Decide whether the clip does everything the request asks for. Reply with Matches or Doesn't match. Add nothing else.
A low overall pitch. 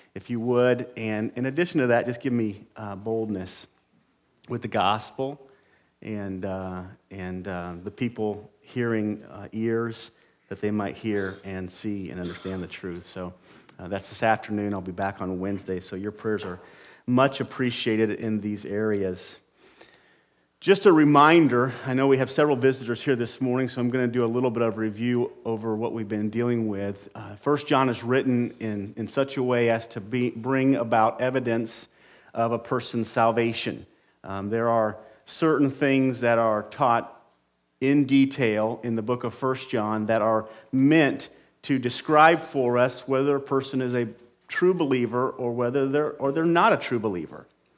Matches